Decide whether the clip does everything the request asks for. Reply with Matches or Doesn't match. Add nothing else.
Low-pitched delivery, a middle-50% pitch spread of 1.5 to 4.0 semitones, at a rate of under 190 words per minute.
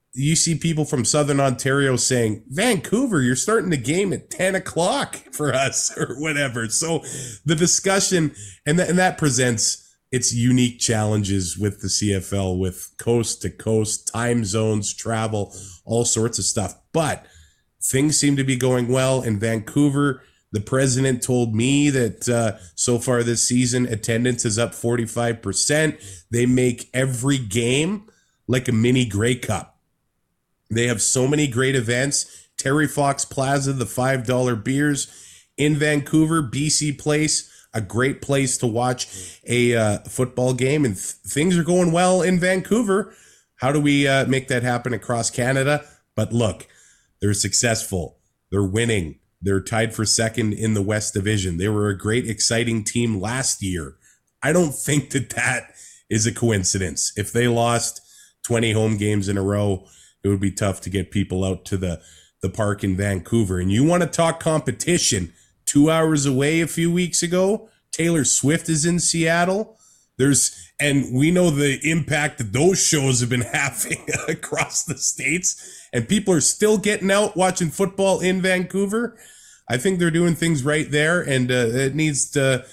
Doesn't match